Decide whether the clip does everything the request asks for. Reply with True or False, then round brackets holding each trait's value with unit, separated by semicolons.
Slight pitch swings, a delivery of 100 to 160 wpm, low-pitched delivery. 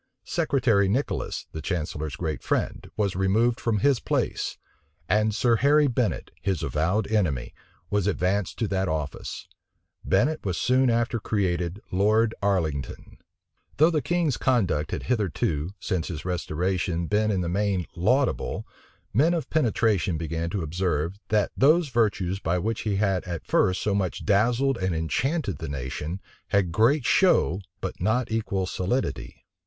False (5.2 semitones; 150 wpm; 100 Hz)